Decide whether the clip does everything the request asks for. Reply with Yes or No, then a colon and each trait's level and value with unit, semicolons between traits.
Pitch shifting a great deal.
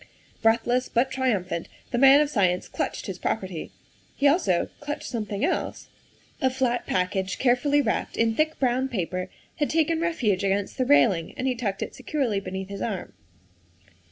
Yes: wide, 5.7 semitones